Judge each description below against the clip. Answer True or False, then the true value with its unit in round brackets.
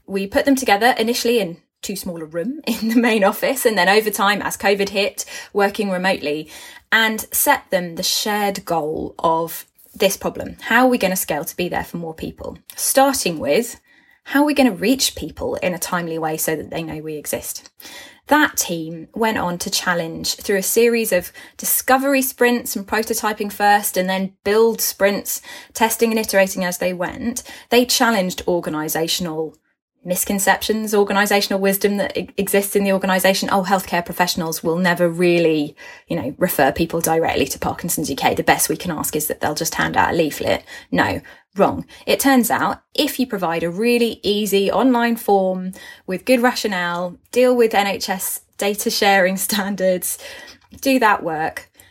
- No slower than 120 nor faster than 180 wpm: True (175 wpm)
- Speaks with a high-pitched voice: True (200 Hz)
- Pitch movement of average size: True (4.6 semitones)